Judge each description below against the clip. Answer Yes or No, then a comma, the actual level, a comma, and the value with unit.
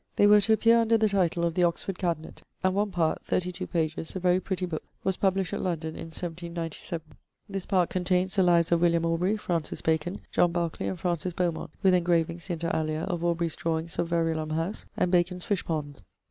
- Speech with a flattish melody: Yes, narrow, 2.1 semitones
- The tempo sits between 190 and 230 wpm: Yes, average, 200 wpm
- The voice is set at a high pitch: No, medium, 175 Hz